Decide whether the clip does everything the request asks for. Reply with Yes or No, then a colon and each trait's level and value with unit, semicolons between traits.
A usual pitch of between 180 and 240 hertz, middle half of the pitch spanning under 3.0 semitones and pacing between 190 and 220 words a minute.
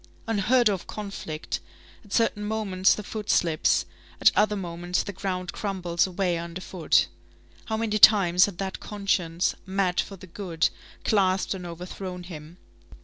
No: high, 190 Hz; narrow, 2.6 semitones; average, 145 wpm